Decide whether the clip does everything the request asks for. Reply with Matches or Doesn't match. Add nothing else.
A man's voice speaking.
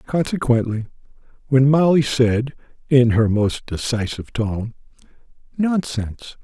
Matches